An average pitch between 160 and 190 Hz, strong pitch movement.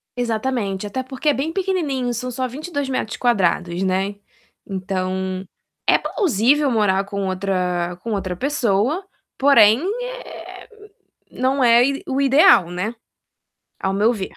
No: high, 230 Hz; wide, 5.9 semitones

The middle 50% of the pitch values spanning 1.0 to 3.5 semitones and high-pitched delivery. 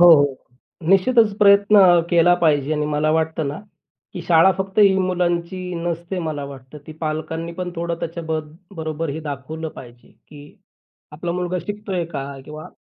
No: average, 2.8 semitones; medium, 170 Hz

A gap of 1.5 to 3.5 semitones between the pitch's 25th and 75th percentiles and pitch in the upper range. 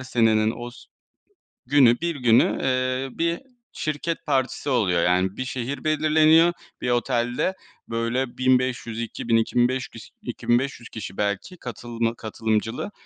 No: average, 2.8 semitones; low, 120 Hz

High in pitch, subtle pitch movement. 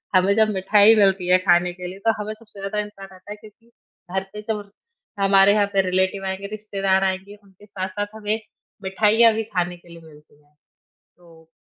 Yes: high, 195 Hz; narrow, 2.1 semitones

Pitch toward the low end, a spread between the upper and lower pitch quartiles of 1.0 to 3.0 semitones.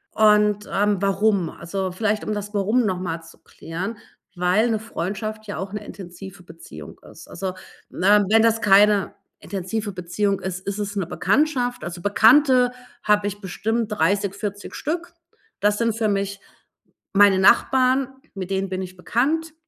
No: high, 205 Hz; narrow, 2.5 semitones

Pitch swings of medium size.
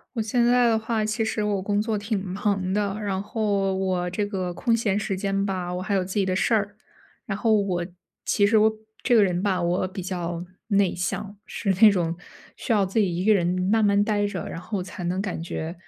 No: narrow, 2.3 semitones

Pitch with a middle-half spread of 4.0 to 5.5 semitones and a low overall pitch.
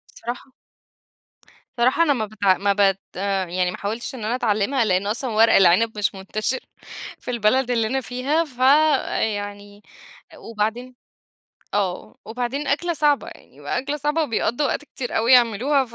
No: average, 4.4 semitones; high, 235 Hz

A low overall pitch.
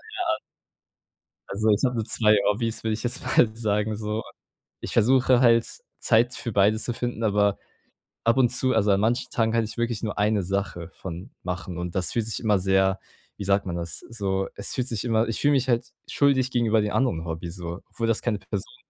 Yes: low, 110 Hz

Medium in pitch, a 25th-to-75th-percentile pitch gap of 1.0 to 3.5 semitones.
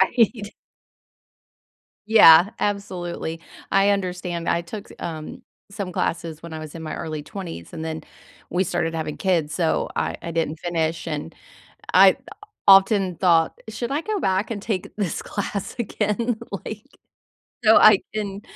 No: medium, 180 Hz; average, 3.9 semitones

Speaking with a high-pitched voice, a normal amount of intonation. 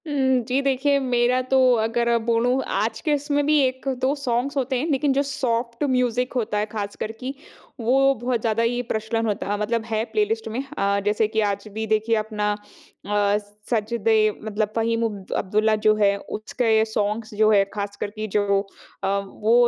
Yes: high, 230 Hz; average, 3.2 semitones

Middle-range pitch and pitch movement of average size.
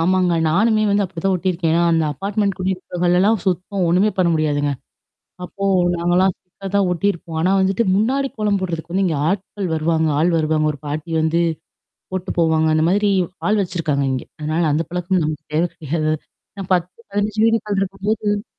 Yes: medium, 180 Hz; average, 3.4 semitones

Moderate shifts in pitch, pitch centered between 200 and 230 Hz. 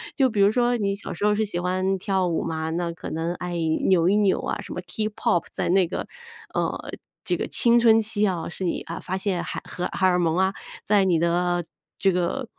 No: average, 3.0 semitones; medium, 185 Hz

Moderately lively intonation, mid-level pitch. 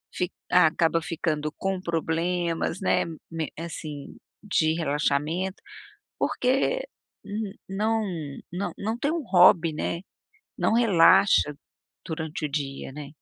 Yes: average, 3.6 semitones; medium, 170 Hz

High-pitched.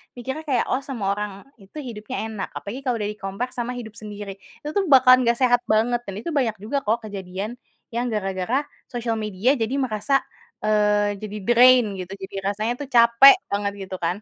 Yes: high, 220 Hz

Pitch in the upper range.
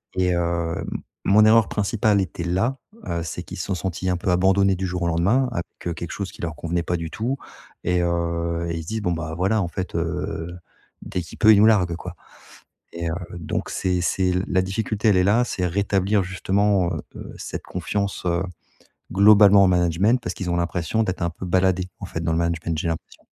No: very low, 90 Hz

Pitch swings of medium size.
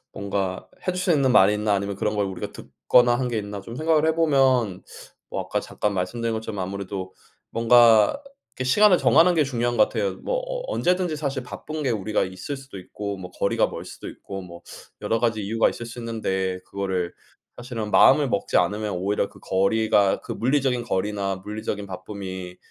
Yes: average, 4.9 semitones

